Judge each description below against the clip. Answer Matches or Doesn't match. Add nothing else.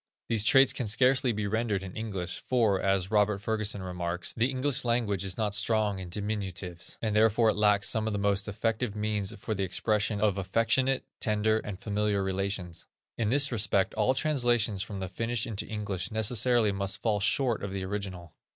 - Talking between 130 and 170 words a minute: Doesn't match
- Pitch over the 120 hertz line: Doesn't match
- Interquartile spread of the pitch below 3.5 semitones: Matches